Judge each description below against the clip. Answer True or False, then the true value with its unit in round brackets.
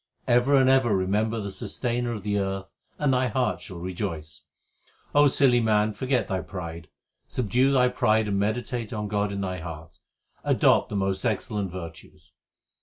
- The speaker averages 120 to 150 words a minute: False (160 wpm)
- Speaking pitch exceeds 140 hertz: False (105 Hz)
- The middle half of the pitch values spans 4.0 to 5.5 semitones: True (4.3 semitones)